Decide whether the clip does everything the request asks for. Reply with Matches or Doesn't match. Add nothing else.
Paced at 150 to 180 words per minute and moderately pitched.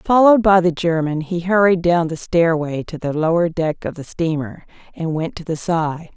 Doesn't match